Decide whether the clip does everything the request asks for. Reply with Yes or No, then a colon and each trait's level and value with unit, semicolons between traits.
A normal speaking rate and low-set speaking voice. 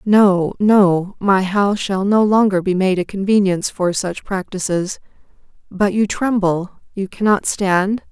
No: average, 150 wpm; high, 195 Hz